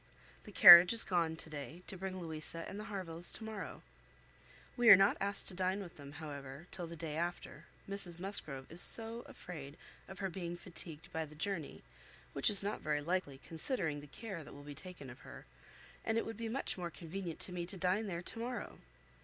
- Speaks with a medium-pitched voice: Yes, medium, 175 Hz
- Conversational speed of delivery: No, fast, 210 wpm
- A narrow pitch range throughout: No, average, 3.8 semitones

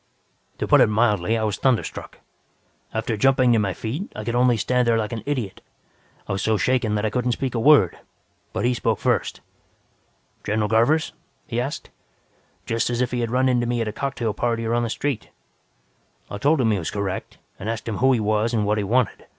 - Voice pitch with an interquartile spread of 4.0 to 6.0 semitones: No, average, 2.7 semitones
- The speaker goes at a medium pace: No, fast, 215 wpm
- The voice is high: No, low, 115 Hz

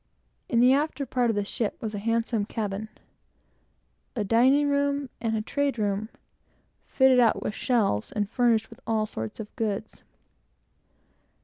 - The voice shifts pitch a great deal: No, average, 3.4 semitones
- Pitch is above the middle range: Yes, high, 225 Hz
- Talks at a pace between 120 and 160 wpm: Yes, average, 150 wpm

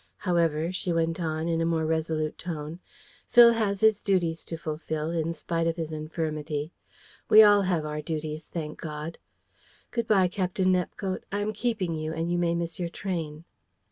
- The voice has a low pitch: No, medium, 165 Hz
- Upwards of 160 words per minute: Yes, average, 175 wpm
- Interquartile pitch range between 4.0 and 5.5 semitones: No, average, 2.8 semitones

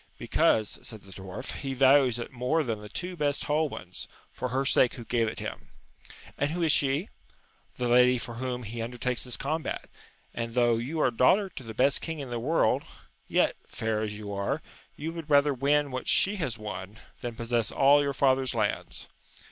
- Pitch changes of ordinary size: Yes, average, 3.8 semitones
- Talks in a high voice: No, low, 125 Hz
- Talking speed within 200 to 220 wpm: Yes, fast, 205 wpm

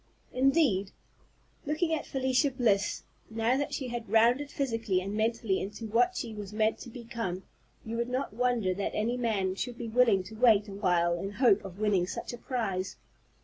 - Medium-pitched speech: No, high, 225 Hz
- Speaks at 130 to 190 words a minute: Yes, average, 185 wpm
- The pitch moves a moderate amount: Yes, average, 3.9 semitones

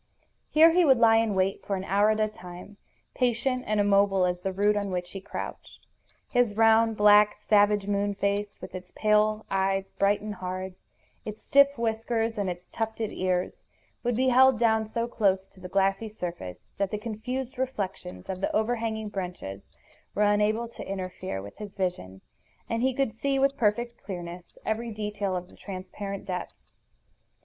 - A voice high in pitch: Yes, high, 210 Hz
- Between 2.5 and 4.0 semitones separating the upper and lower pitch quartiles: Yes, average, 2.9 semitones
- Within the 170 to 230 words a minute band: Yes, average, 175 wpm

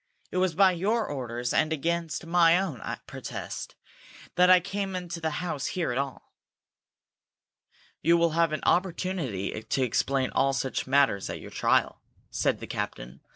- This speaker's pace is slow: No, average, 155 wpm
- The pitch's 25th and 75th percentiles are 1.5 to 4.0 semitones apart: No, average, 5.1 semitones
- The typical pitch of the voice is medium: Yes, medium, 165 Hz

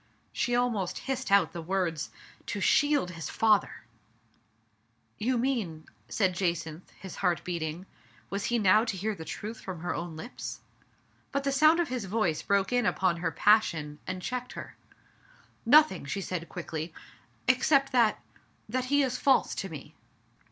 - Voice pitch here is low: No, high, 200 Hz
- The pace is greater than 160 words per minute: Yes, average, 170 wpm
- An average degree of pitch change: No, wide, 6.4 semitones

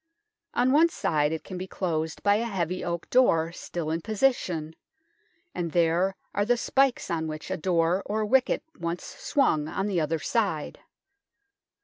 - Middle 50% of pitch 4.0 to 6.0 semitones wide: Yes, average, 5.1 semitones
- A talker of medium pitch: Yes, medium, 180 Hz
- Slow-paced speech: No, average, 160 wpm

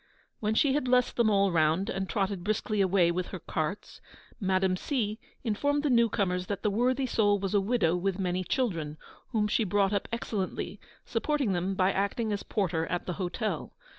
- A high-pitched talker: Yes, high, 200 Hz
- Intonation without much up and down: No, average, 3.5 semitones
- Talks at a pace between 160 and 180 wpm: No, average, 190 wpm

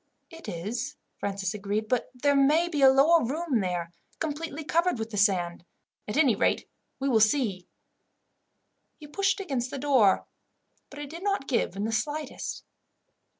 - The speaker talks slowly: No, average, 160 wpm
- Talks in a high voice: Yes, very high, 270 Hz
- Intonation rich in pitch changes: Yes, wide, 6.4 semitones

